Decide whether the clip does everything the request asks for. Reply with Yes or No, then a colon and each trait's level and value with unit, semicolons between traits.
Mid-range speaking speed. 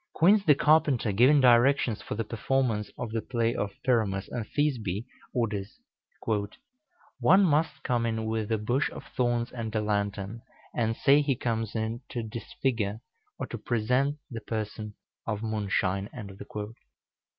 Yes: average, 145 wpm